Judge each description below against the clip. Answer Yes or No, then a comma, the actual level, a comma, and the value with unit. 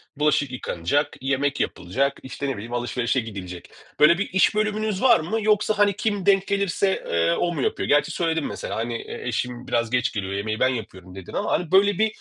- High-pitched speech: No, medium, 140 Hz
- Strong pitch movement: Yes, wide, 9.0 semitones